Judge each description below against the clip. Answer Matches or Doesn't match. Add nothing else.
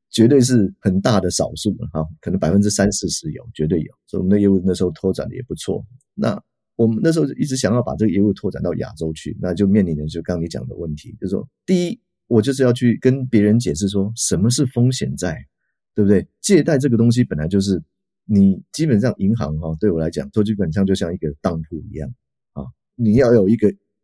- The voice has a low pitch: Matches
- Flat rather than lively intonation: Doesn't match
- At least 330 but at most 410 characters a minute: Matches